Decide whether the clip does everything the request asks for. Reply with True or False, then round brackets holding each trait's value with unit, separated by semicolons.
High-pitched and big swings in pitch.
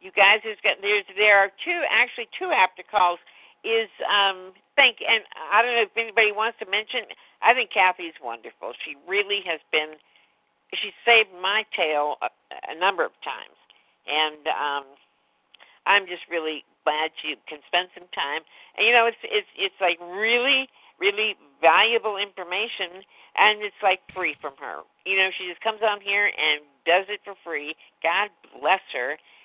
False (200 Hz; 4.5 semitones)